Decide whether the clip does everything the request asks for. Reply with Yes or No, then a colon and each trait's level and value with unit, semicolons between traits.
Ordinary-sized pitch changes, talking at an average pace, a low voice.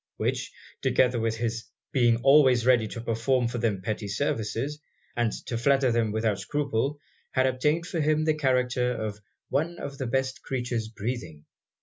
Yes: average, 3.4 semitones; average, 160 wpm; low, 125 Hz